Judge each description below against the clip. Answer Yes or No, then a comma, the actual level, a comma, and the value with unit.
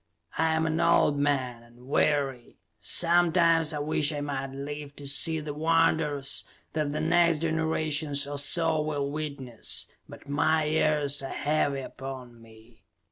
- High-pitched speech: No, medium, 145 Hz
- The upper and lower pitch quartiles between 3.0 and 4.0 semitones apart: No, narrow, 2.4 semitones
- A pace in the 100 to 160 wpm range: Yes, average, 145 wpm